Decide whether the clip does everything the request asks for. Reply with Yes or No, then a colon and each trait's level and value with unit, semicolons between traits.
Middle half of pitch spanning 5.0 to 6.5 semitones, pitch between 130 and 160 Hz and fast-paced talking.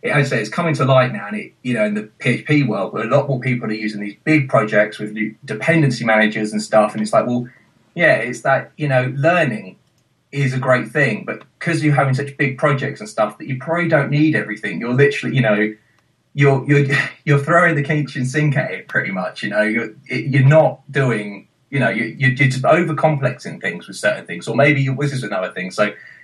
Yes: average, 5.3 semitones; low, 135 Hz; fast, 225 wpm